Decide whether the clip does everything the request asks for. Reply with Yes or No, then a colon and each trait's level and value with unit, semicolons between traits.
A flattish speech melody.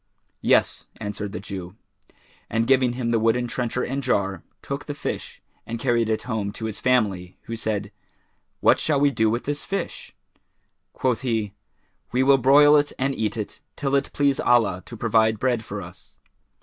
No: average, 3.6 semitones